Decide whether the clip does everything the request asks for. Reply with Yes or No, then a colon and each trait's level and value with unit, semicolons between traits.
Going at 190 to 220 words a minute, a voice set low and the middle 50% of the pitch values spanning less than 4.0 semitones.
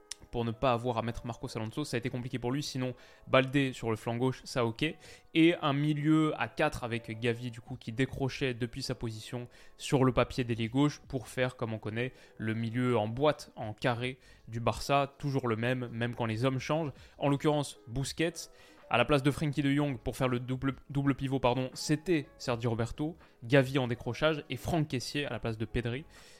Yes: average, 210 wpm; low, 130 Hz; average, 3.0 semitones